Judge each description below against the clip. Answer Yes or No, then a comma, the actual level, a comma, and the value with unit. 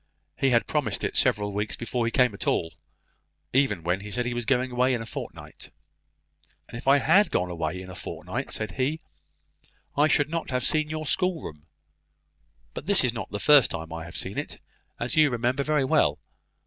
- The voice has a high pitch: No, low, 125 Hz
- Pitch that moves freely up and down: Yes, wide, 5.7 semitones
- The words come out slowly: No, average, 200 wpm